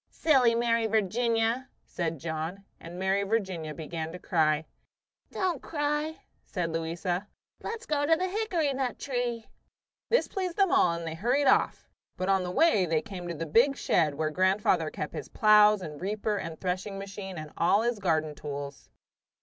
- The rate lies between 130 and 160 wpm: No, average, 170 wpm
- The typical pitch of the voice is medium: No, high, 195 Hz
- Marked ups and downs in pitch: Yes, wide, 6.7 semitones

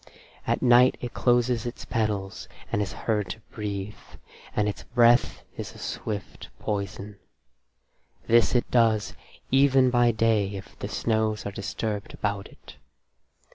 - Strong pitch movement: No, average, 2.8 semitones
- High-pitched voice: No, low, 110 Hz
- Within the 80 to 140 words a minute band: Yes, slow, 135 wpm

